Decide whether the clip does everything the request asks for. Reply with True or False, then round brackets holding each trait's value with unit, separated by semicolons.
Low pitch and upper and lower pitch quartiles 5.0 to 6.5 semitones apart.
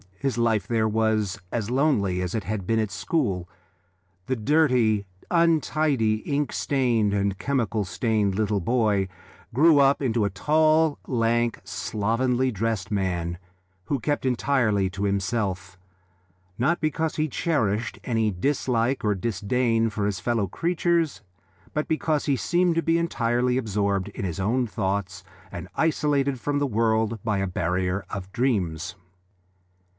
True (115 Hz; 5.4 semitones)